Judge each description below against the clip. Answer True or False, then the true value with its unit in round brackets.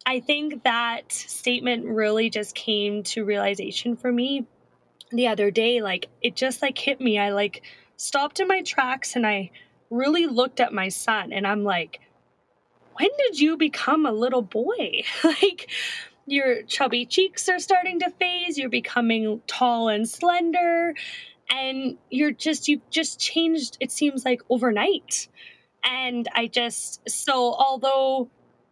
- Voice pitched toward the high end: True (255 Hz)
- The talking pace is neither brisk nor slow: True (150 wpm)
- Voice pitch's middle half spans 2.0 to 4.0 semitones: False (5.2 semitones)